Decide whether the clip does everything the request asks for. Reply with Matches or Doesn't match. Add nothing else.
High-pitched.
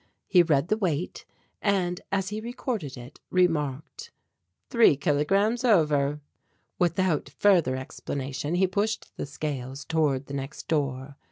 Doesn't match